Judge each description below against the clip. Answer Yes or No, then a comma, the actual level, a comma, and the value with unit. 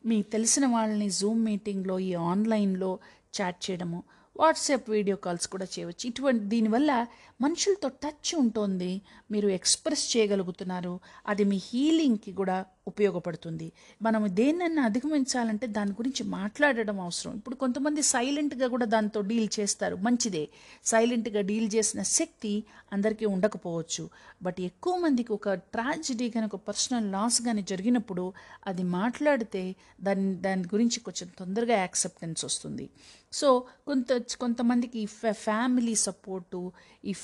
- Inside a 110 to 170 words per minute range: Yes, average, 120 wpm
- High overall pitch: Yes, high, 215 Hz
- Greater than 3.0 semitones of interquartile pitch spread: Yes, average, 4.3 semitones